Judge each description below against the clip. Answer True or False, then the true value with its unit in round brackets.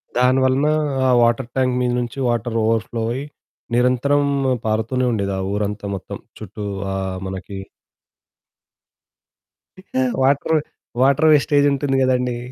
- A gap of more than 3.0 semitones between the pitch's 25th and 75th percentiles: True (3.4 semitones)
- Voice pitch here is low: True (125 Hz)